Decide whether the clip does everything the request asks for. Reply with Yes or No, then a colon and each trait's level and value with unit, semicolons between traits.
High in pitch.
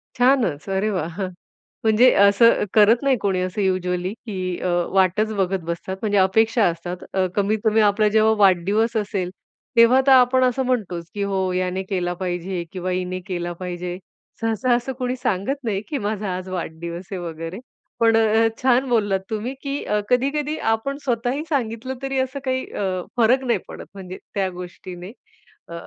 Yes: high, 205 Hz